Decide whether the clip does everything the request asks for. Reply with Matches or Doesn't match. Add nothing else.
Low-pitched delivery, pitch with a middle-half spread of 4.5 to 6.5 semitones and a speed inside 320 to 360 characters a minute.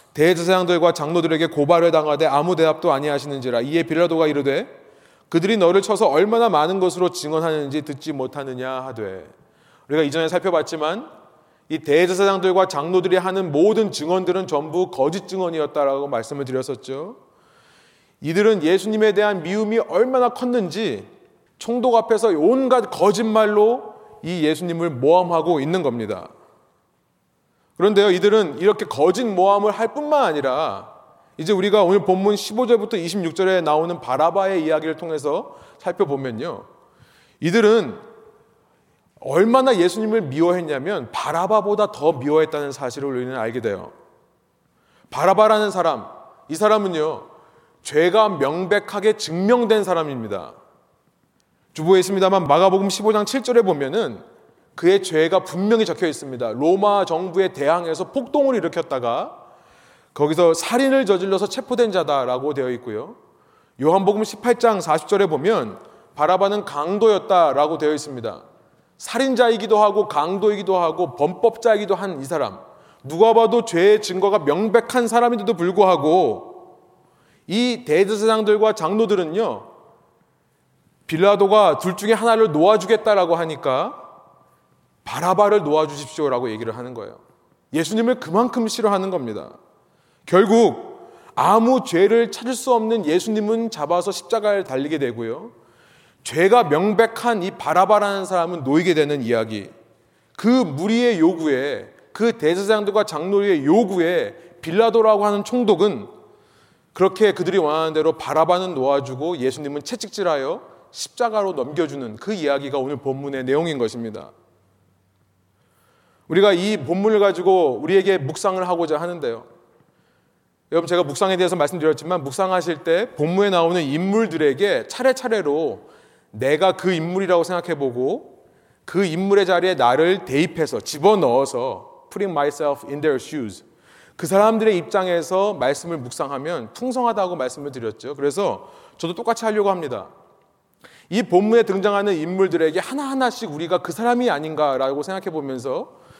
Doesn't match